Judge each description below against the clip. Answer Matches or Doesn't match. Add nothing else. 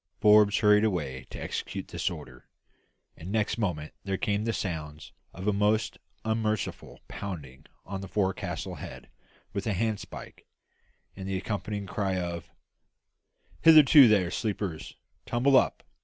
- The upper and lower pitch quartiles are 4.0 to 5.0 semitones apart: Doesn't match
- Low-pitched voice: Matches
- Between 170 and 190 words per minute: Doesn't match